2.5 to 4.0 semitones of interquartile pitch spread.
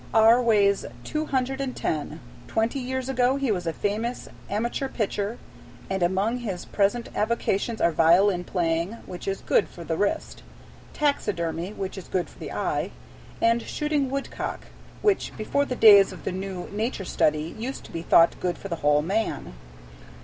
No: wide, 5.6 semitones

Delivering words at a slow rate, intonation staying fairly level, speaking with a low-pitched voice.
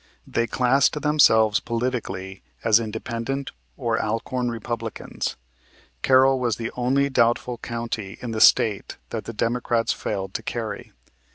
Yes: slow, 125 wpm; narrow, 2.2 semitones; low, 115 Hz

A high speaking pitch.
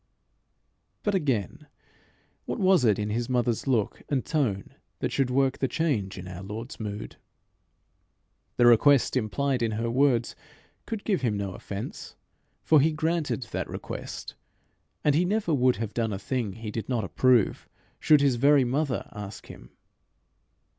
No: low, 125 Hz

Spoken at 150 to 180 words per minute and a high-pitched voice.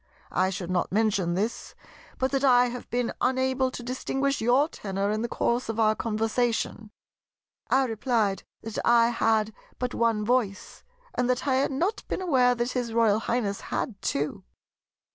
Yes: average, 165 wpm; high, 235 Hz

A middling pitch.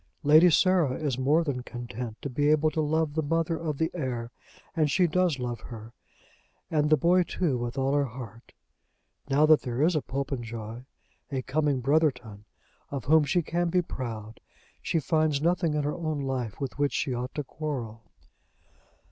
Yes: medium, 145 Hz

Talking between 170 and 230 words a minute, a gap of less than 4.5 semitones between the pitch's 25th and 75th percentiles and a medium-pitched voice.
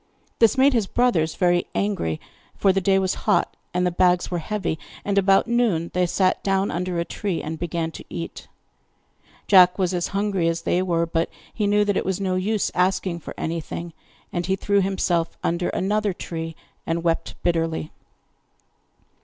Yes: average, 180 wpm; average, 2.7 semitones; medium, 180 Hz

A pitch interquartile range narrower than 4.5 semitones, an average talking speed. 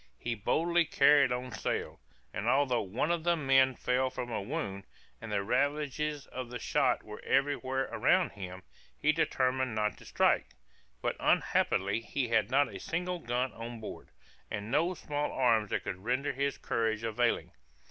Yes: average, 4.1 semitones; average, 170 wpm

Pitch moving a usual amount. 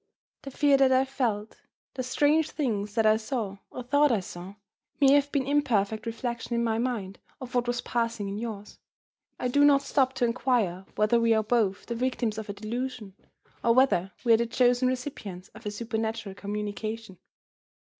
Yes: average, 3.5 semitones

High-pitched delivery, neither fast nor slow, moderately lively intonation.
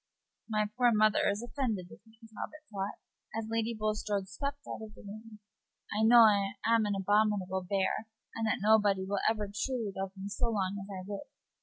No: high, 210 Hz; average, 190 wpm; narrow, 2.1 semitones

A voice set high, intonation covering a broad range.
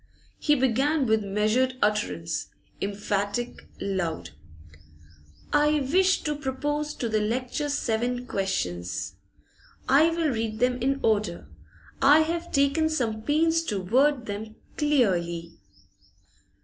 Yes: high, 245 Hz; wide, 6.3 semitones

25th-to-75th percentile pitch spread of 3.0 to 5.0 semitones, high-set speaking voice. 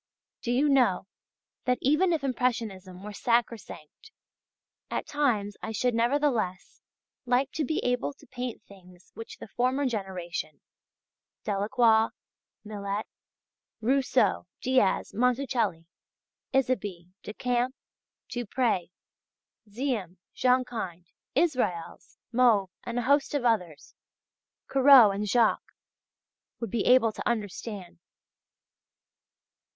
Yes: average, 4.3 semitones; high, 235 Hz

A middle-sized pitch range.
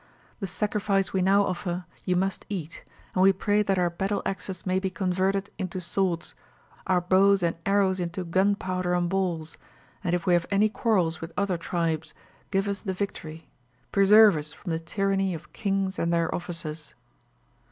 No: narrow, 2.3 semitones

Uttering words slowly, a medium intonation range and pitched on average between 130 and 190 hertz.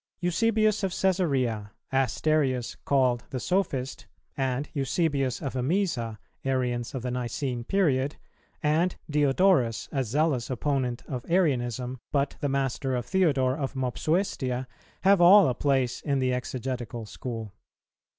Yes: slow, 125 wpm; average, 3.8 semitones; low, 135 Hz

